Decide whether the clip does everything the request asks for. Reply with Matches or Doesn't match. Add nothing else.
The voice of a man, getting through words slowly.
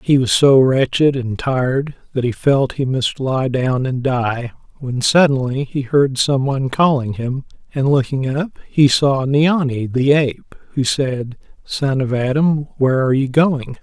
Doesn't match